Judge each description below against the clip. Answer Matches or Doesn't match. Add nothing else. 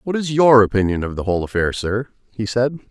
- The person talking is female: Doesn't match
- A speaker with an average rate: Doesn't match